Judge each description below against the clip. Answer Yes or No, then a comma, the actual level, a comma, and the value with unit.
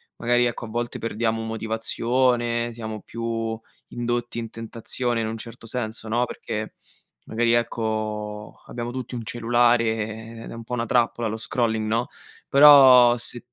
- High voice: No, low, 115 Hz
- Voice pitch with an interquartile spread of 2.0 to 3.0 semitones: No, narrow, 1.3 semitones